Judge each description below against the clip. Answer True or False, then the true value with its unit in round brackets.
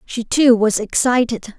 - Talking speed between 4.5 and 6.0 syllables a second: False (4.1 syllables/s)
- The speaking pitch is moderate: False (230 Hz)